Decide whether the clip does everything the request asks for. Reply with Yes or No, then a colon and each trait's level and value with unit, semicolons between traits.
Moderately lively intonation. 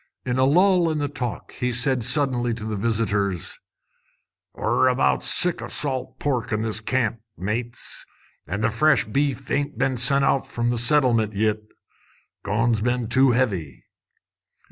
Yes: average, 3.6 semitones